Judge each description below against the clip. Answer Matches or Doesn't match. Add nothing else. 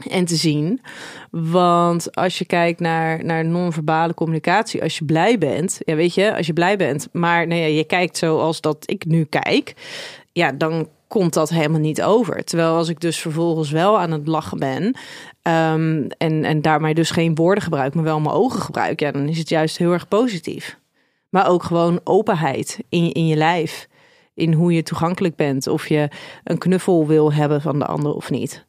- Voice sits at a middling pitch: Matches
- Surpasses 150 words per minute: Matches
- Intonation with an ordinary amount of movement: Doesn't match